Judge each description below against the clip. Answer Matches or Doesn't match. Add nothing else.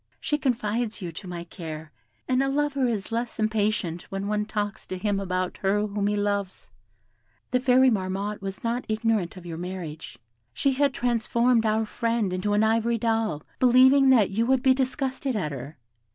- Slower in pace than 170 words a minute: Doesn't match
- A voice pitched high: Matches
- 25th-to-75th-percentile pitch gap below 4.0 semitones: Doesn't match